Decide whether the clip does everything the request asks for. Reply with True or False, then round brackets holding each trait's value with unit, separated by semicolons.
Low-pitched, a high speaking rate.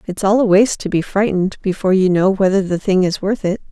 False (195 Hz; 240 wpm)